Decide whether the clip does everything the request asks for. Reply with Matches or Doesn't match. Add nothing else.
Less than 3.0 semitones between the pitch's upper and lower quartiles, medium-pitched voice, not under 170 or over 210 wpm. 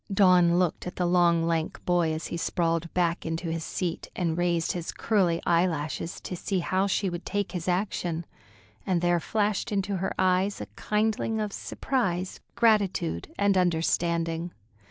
Doesn't match